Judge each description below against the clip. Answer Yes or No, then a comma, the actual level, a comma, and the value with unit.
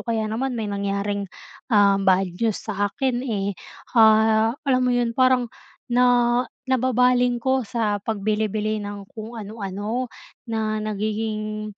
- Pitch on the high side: Yes, high, 220 Hz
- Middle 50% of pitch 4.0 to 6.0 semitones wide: No, average, 2.9 semitones